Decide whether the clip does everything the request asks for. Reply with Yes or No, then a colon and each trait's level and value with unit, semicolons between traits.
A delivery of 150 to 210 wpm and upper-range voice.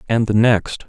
No: fast, 205 wpm; low, 110 Hz